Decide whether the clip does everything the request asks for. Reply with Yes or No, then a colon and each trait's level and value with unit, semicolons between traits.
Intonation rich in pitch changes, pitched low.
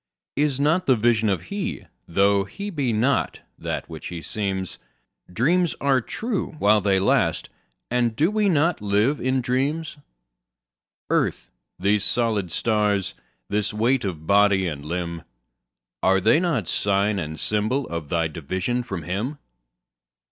Yes: wide, 6.8 semitones; low, 105 Hz